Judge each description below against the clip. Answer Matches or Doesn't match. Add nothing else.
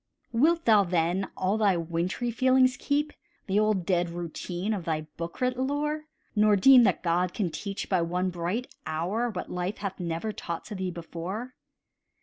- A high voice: Matches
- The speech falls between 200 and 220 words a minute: Doesn't match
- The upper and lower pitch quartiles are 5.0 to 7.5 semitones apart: Matches